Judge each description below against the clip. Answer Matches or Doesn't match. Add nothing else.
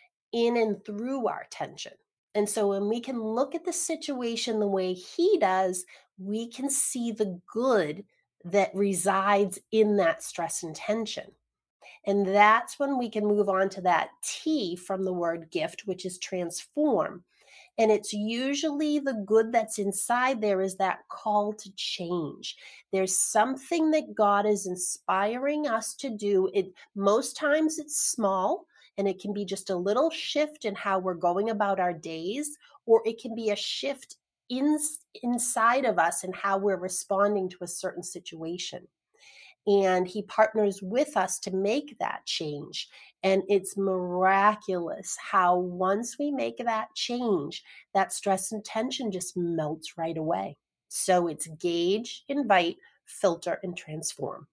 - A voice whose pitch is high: Matches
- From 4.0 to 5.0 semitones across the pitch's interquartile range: Matches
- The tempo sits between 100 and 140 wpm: Doesn't match